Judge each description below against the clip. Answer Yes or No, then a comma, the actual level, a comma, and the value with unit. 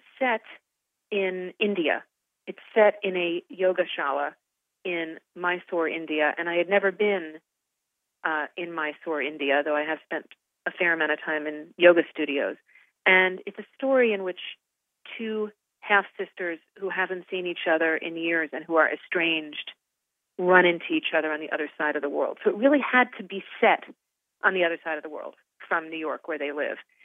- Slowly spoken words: No, average, 185 wpm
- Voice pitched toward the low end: No, medium, 175 Hz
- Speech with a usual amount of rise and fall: Yes, average, 3.7 semitones